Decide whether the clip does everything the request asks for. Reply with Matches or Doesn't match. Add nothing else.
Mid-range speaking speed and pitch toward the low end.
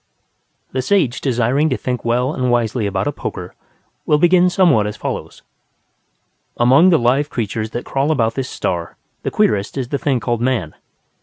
Matches